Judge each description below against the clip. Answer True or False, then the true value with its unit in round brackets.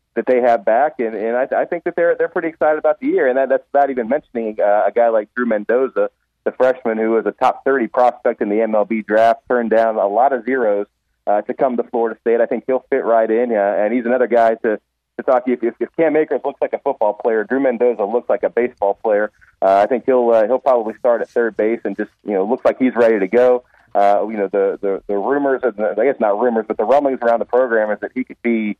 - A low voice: True (120 Hz)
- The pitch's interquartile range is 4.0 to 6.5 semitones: False (2.9 semitones)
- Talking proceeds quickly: True (265 wpm)